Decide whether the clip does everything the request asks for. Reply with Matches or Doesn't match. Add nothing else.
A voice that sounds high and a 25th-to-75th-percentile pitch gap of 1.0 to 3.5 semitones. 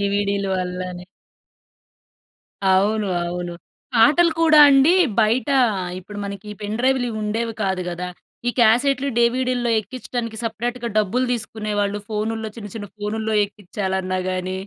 Matches